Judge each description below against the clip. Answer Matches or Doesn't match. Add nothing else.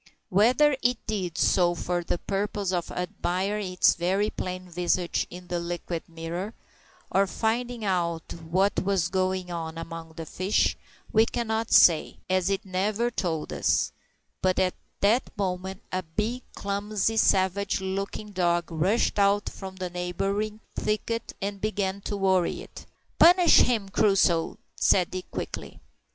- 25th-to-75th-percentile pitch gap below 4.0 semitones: Matches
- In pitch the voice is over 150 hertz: Matches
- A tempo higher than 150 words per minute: Doesn't match